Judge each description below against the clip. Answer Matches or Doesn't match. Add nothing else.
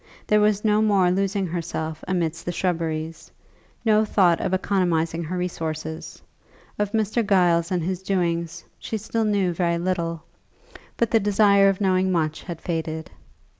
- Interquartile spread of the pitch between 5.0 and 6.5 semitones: Doesn't match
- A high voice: Doesn't match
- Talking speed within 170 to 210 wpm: Doesn't match